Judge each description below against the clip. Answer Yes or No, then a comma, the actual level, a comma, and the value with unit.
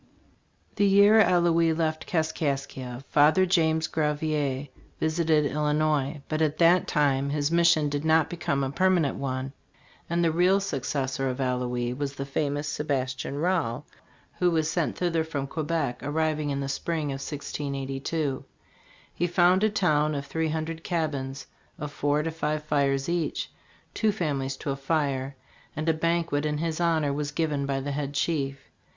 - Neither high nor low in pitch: Yes, medium, 150 Hz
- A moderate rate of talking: Yes, average, 160 wpm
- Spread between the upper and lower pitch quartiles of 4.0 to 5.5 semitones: No, average, 2.9 semitones